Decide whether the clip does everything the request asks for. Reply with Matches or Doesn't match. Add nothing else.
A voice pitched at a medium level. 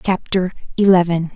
Matches